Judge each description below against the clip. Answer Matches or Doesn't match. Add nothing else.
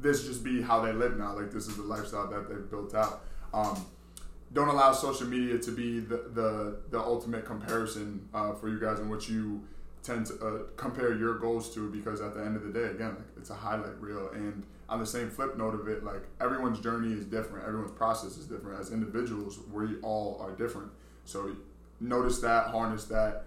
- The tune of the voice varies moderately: Doesn't match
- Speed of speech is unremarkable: Doesn't match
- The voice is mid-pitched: Doesn't match